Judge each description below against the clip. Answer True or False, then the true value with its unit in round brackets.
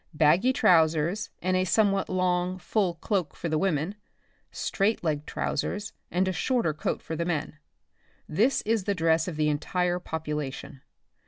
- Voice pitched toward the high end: False (175 Hz)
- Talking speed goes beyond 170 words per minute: False (160 wpm)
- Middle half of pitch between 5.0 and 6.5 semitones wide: False (3.7 semitones)